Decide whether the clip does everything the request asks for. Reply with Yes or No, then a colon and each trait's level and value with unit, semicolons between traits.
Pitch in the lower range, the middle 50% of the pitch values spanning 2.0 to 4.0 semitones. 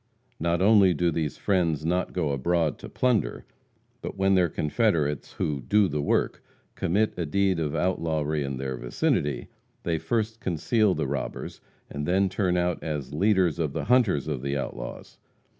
No: very low, 85 Hz; average, 4.6 semitones